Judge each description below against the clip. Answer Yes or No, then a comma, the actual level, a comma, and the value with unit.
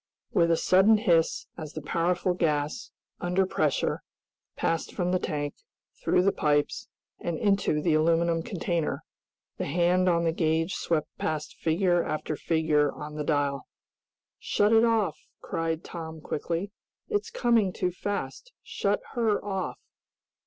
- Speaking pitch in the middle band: Yes, medium, 170 Hz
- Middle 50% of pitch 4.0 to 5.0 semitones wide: No, average, 3.3 semitones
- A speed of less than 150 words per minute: Yes, average, 140 wpm